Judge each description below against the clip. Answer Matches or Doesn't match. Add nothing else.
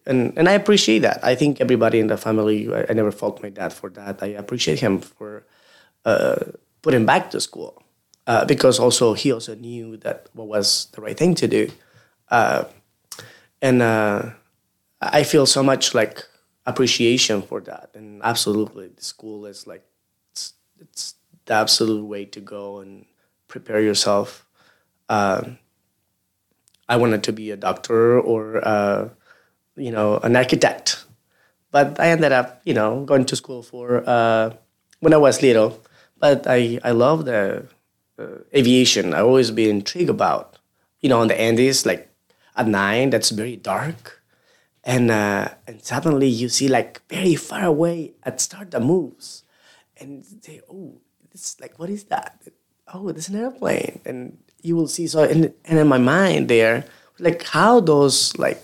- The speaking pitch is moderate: Doesn't match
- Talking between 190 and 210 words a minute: Doesn't match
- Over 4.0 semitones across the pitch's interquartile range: Matches